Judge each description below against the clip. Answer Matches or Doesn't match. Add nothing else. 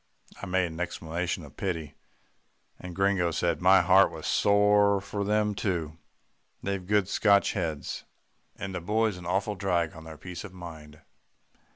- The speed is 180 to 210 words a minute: Doesn't match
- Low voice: Matches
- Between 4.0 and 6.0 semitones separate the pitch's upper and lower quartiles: Doesn't match